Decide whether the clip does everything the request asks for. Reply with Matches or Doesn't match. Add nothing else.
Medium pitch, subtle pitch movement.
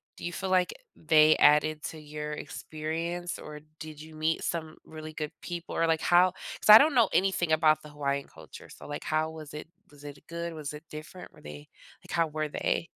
Matches